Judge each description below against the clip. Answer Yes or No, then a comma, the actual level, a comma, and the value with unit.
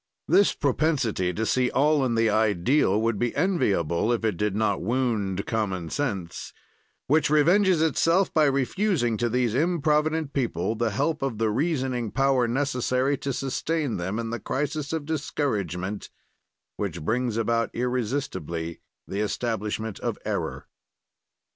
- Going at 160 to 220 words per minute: No, average, 140 wpm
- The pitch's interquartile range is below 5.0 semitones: No, average, 5.3 semitones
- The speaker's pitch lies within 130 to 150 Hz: No, low, 120 Hz